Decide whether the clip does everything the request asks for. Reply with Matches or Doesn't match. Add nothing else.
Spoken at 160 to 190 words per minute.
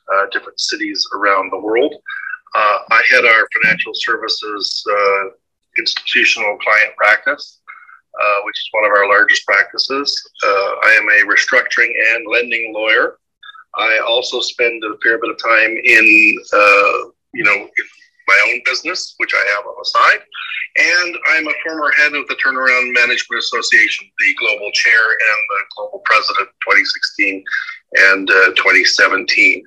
Doesn't match